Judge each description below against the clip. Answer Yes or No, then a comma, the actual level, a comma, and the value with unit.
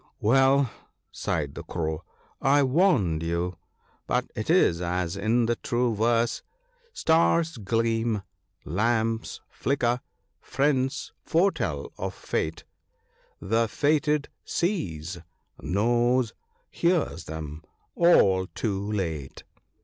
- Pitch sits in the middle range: No, low, 115 Hz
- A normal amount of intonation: No, wide, 7.5 semitones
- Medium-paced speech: No, slow, 110 wpm